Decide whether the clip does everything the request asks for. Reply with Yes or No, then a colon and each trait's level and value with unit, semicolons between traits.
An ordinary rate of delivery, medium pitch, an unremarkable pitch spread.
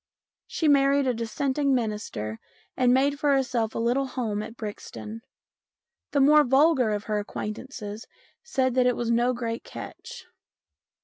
No: average, 145 wpm; very high, 250 Hz; average, 3.6 semitones